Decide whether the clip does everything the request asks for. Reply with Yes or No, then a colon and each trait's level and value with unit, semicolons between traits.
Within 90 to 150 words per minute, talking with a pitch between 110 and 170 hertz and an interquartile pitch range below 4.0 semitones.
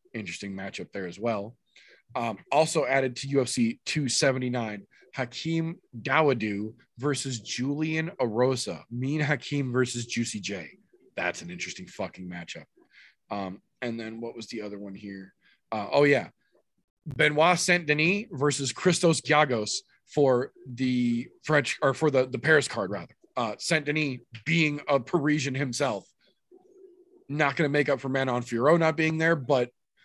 No: average, 145 wpm; low, 135 Hz; average, 4.7 semitones